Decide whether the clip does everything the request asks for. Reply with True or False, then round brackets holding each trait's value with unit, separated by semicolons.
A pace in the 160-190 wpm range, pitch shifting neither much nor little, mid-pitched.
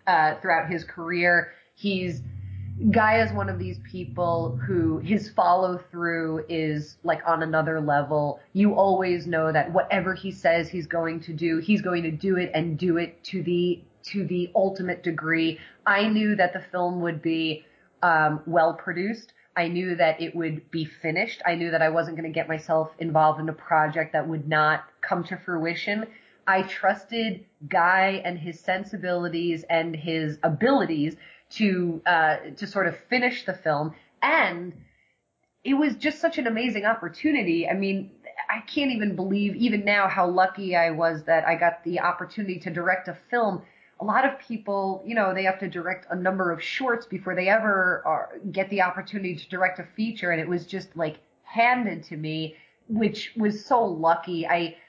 True (180 wpm; 3.0 semitones; 175 Hz)